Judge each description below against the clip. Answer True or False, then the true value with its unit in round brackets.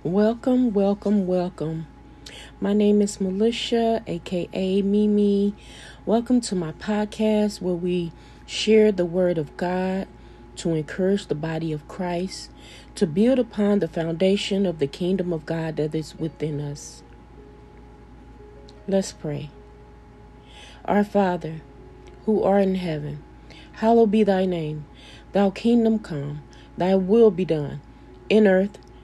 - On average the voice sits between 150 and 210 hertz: True (185 Hz)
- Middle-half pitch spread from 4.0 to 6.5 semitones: True (4.8 semitones)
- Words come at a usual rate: False (125 wpm)